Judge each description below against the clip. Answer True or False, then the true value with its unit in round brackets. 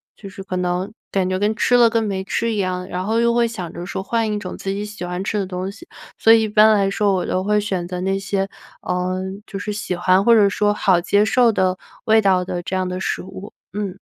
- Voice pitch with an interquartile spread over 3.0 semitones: False (2.4 semitones)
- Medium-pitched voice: False (195 Hz)